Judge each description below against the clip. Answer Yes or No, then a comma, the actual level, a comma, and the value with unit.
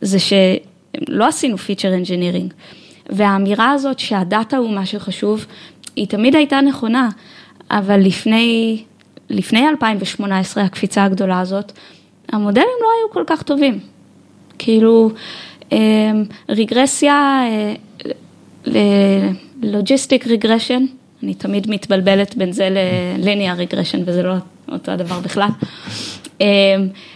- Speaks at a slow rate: Yes, slow, 95 wpm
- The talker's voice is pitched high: Yes, high, 205 Hz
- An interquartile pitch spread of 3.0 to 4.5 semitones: Yes, average, 3.4 semitones